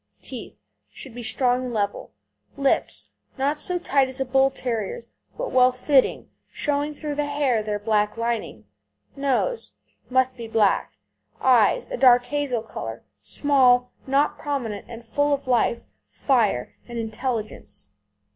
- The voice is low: No, very high, 250 Hz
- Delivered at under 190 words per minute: Yes, average, 140 wpm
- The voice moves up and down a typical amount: Yes, average, 3.7 semitones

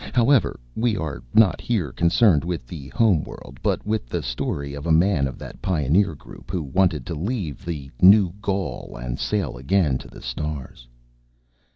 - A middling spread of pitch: No, wide, 5.9 semitones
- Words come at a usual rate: Yes, average, 175 wpm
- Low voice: Yes, very low, 85 Hz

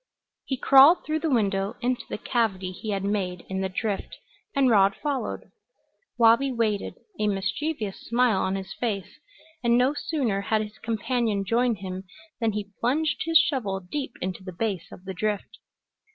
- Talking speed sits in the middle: Yes, average, 165 wpm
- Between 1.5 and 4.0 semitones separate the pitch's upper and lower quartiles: No, average, 4.4 semitones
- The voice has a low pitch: No, high, 215 Hz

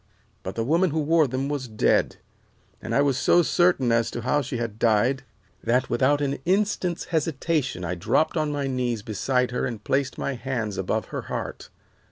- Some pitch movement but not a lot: Yes, average, 4.0 semitones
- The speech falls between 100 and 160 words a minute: No, average, 190 wpm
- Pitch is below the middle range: Yes, low, 130 Hz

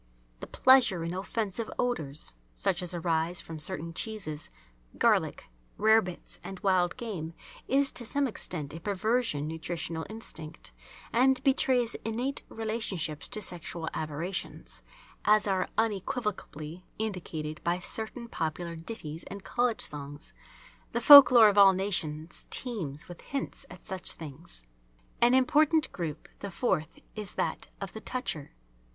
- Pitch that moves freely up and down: Yes, wide, 5.8 semitones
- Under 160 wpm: Yes, slow, 135 wpm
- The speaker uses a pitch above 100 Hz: Yes, high, 190 Hz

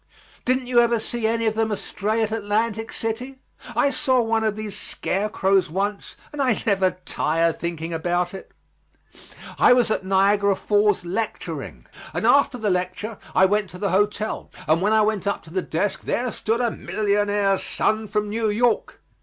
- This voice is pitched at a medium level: No, high, 210 Hz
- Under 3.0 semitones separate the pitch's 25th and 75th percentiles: Yes, narrow, 2.6 semitones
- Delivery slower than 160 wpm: No, average, 180 wpm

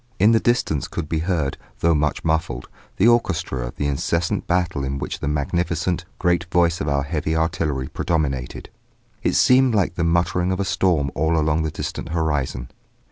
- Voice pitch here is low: Yes, very low, 80 Hz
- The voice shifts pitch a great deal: No, average, 3.1 semitones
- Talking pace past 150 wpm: Yes, average, 180 wpm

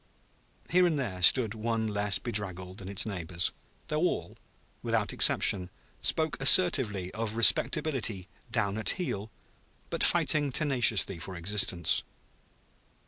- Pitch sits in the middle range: No, low, 105 Hz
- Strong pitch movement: Yes, wide, 5.8 semitones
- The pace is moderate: No, slow, 125 wpm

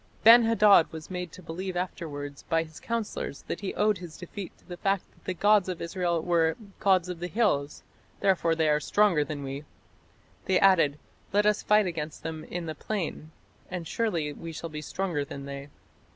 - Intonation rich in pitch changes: No, average, 3.8 semitones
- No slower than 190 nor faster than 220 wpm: Yes, average, 195 wpm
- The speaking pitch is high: No, medium, 175 Hz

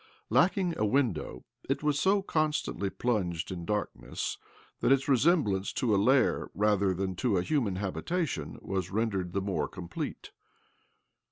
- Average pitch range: No, wide, 6.9 semitones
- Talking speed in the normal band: Yes, average, 145 wpm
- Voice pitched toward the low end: Yes, low, 105 Hz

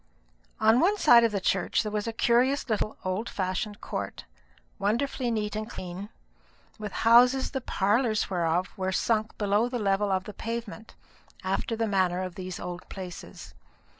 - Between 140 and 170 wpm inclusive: Yes, average, 165 wpm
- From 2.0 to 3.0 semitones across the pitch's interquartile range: No, average, 3.6 semitones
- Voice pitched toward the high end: Yes, high, 210 Hz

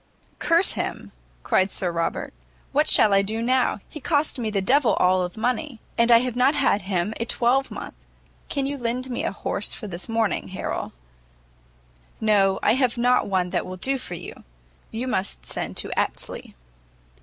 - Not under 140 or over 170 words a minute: No, average, 185 wpm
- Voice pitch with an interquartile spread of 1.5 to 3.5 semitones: No, average, 4.6 semitones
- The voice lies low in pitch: No, high, 230 Hz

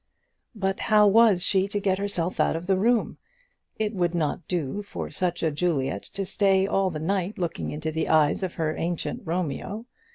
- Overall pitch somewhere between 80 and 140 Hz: No, medium, 185 Hz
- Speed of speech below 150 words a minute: No, average, 190 wpm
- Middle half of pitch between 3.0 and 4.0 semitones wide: Yes, average, 3.4 semitones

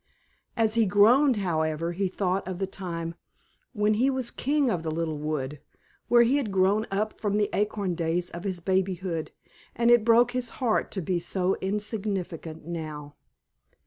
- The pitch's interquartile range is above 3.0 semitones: Yes, average, 4.5 semitones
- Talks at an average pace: Yes, average, 170 wpm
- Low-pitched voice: No, high, 195 Hz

